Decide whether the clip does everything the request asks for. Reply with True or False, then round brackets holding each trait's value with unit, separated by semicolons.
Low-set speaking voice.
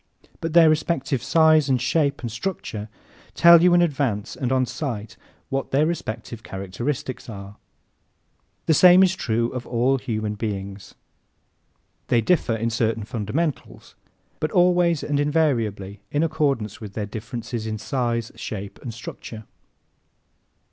True (125 Hz)